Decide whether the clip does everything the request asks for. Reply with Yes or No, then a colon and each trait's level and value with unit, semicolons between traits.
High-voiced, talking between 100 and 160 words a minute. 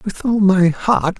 No: high, 195 Hz; average, 200 wpm